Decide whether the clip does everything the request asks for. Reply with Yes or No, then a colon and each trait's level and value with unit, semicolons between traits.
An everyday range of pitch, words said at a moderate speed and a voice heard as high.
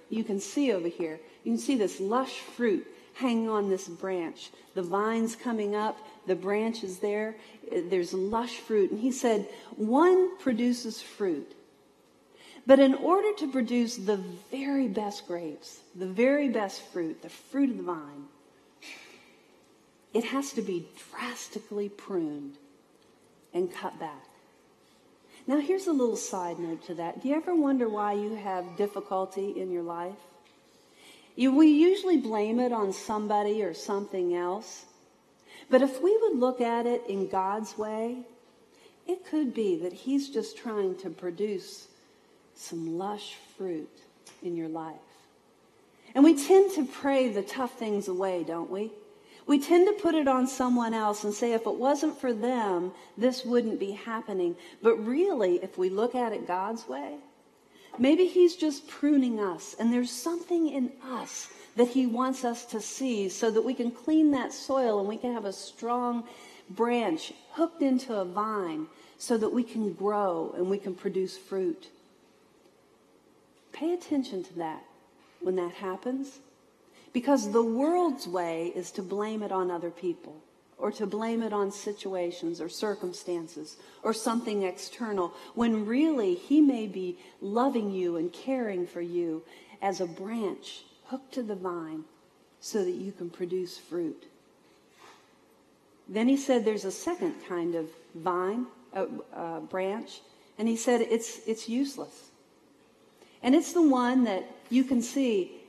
No: wide, 5.8 semitones; average, 155 wpm; high, 225 Hz